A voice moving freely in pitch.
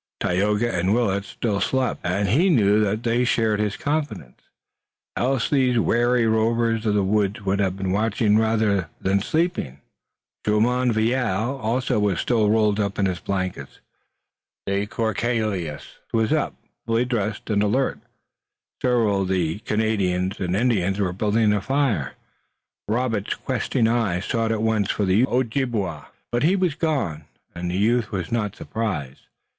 No: average, 3.4 semitones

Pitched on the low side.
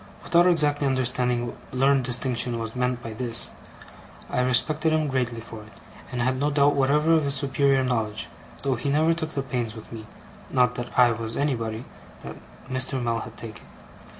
Yes: low, 125 Hz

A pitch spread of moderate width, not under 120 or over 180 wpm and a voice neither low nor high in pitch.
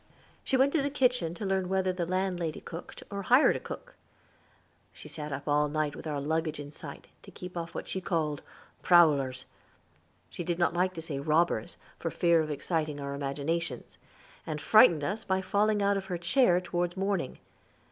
No: average, 4.0 semitones; average, 190 wpm; medium, 170 Hz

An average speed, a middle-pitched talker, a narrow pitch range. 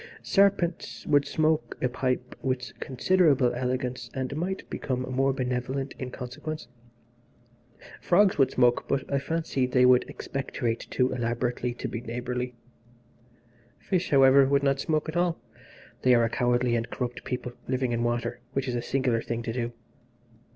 No: average, 155 wpm; low, 130 Hz; narrow, 2.2 semitones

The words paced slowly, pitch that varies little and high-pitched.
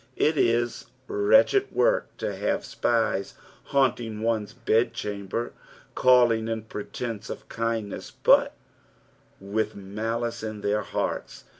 No: slow, 110 wpm; narrow, 2.2 semitones; low, 115 Hz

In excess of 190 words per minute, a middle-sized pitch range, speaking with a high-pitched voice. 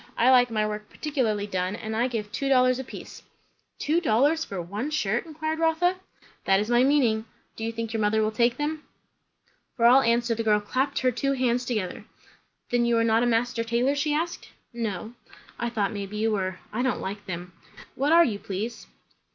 Yes: average, 200 wpm; average, 3.8 semitones; high, 235 Hz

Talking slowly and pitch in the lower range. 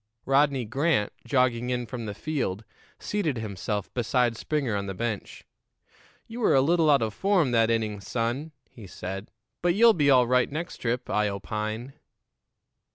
No: average, 160 wpm; low, 125 Hz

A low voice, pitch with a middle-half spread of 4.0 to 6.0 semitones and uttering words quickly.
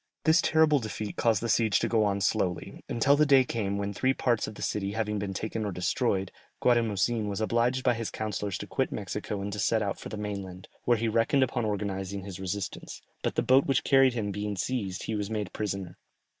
No: low, 105 Hz; average, 3.1 semitones; fast, 220 wpm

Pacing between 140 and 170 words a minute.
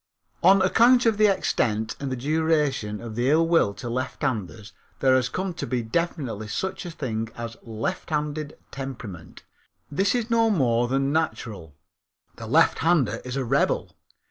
Yes: average, 160 wpm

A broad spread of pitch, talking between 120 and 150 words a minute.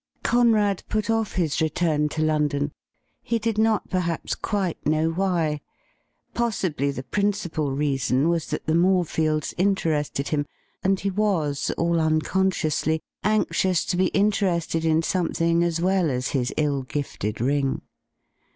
No: average, 4.2 semitones; average, 140 wpm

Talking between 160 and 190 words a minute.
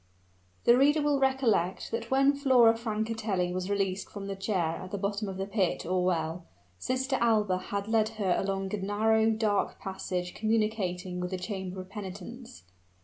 Yes: average, 170 wpm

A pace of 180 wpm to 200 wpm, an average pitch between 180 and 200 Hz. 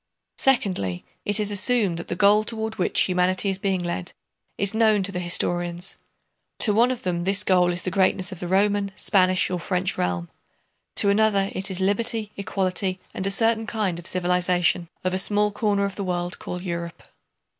Yes: average, 190 wpm; high, 190 Hz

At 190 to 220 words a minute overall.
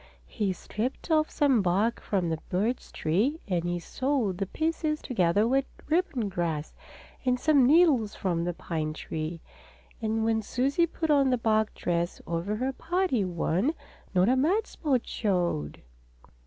No: average, 155 wpm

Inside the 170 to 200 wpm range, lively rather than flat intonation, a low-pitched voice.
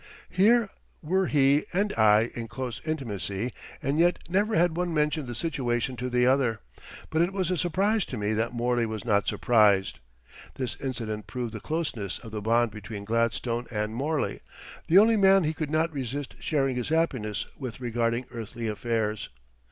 Yes: average, 175 wpm; wide, 6.0 semitones; low, 125 Hz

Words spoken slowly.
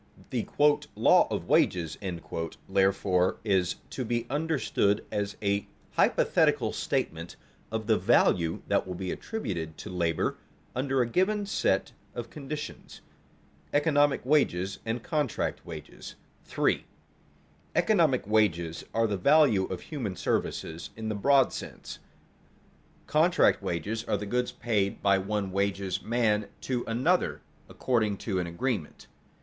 Yes: slow, 130 wpm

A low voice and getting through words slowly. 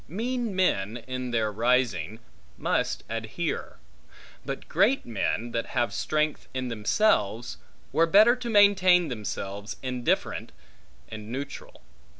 Yes: low, 125 Hz; slow, 115 wpm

